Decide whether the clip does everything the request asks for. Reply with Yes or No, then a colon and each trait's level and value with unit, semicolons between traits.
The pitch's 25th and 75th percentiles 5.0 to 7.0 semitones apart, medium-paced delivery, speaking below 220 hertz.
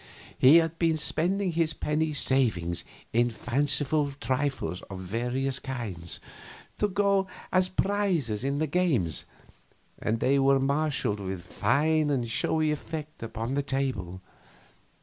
No: wide, 5.4 semitones; slow, 130 wpm; medium, 140 Hz